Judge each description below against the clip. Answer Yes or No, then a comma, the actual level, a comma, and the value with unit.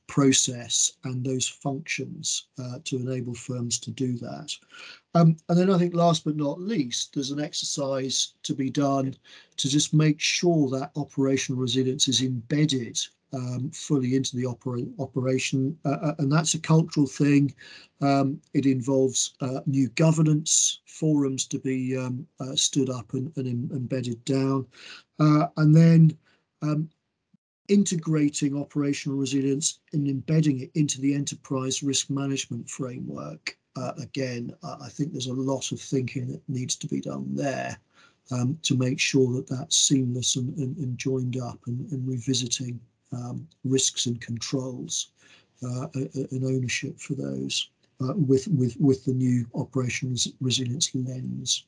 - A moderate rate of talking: Yes, average, 150 wpm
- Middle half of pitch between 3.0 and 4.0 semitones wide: No, narrow, 2.5 semitones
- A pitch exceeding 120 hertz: Yes, low, 135 Hz